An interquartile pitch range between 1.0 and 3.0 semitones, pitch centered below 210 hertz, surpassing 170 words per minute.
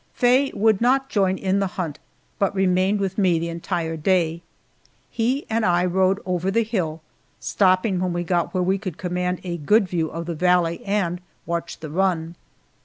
Yes: narrow, 2.5 semitones; medium, 185 Hz; average, 180 wpm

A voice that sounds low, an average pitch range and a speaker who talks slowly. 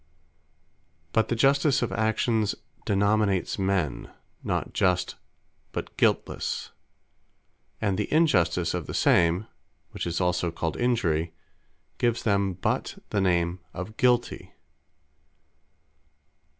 Yes: low, 100 Hz; average, 4.1 semitones; slow, 105 wpm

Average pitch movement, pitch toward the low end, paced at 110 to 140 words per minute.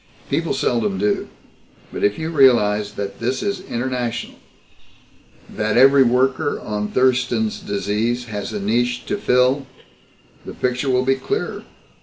Yes: average, 3.9 semitones; low, 125 Hz; slow, 135 wpm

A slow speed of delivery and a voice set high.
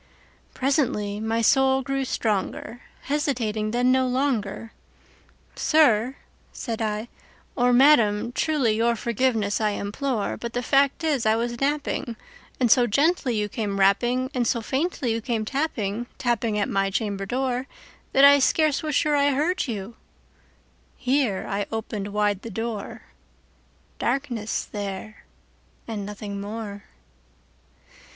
Yes: slow, 120 wpm; high, 235 Hz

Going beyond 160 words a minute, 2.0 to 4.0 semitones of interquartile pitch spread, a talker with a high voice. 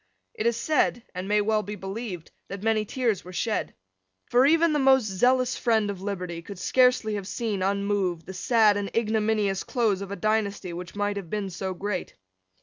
Yes: average, 190 wpm; average, 2.8 semitones; high, 205 Hz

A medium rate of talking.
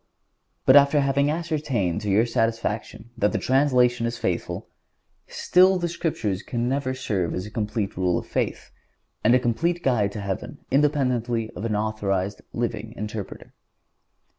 Yes: average, 150 wpm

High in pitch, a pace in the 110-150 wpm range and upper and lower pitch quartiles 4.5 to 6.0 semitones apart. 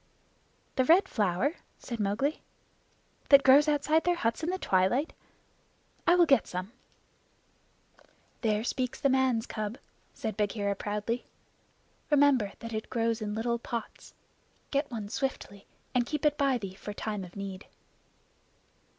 Yes: high, 235 Hz; average, 140 wpm; average, 5.2 semitones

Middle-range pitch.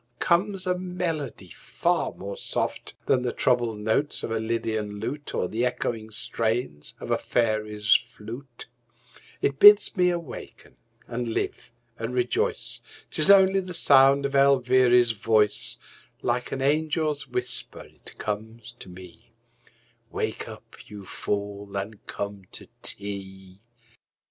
No: low, 120 Hz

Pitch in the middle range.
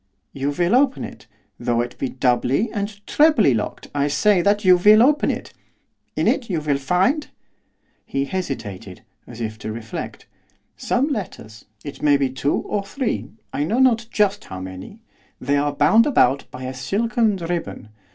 Yes: medium, 165 Hz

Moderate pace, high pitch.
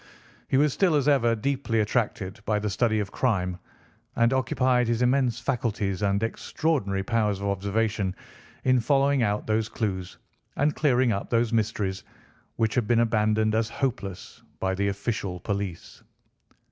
No: average, 150 wpm; low, 110 Hz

